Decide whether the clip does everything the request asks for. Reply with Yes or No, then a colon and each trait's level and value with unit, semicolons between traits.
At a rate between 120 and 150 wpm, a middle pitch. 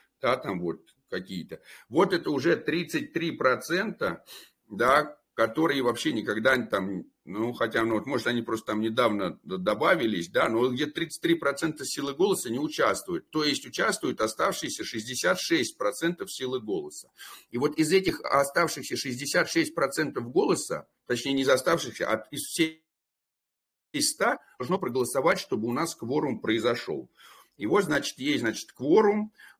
Yes: average, 135 wpm; medium, 150 Hz